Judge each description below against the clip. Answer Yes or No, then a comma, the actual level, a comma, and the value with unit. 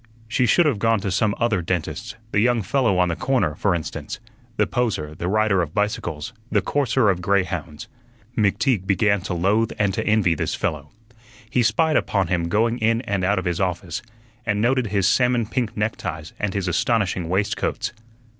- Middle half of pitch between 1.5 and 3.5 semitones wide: No, average, 4.1 semitones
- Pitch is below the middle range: Yes, low, 100 Hz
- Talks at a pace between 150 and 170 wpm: No, average, 185 wpm